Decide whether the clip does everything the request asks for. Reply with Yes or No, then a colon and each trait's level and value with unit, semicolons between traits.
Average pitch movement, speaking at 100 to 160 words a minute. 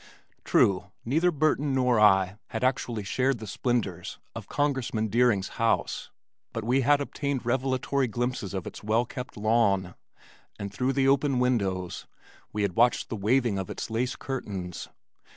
Yes: average, 4.4 semitones; average, 150 wpm